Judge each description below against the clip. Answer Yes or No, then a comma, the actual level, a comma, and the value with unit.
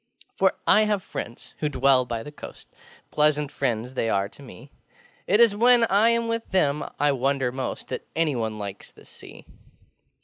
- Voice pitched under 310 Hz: Yes, medium, 140 Hz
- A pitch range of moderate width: No, wide, 7.9 semitones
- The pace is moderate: Yes, average, 175 wpm